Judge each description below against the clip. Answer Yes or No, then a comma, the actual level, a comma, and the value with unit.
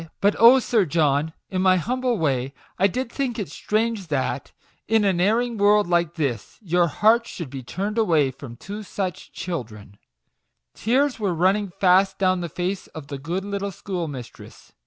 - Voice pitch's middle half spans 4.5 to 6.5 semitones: Yes, average, 5.1 semitones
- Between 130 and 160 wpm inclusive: No, average, 175 wpm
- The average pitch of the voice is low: No, medium, 185 Hz